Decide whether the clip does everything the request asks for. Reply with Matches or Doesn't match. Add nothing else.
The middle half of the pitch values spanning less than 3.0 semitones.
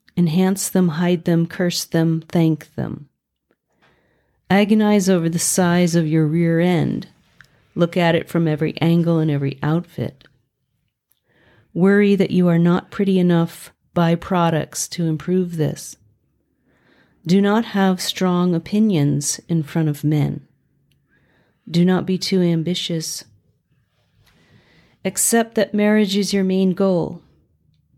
Matches